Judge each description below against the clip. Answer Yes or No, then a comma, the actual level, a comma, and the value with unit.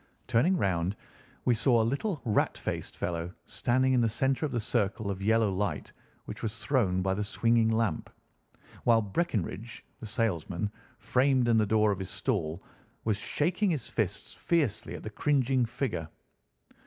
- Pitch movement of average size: Yes, average, 4.2 semitones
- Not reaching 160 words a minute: No, average, 165 wpm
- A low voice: Yes, low, 115 Hz